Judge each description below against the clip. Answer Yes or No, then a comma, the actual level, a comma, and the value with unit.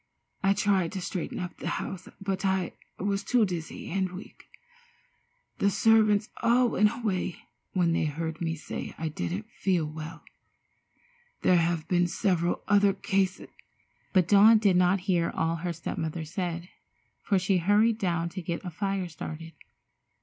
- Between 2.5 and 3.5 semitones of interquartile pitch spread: Yes, average, 3.0 semitones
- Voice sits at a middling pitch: Yes, medium, 180 Hz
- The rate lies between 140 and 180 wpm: Yes, average, 160 wpm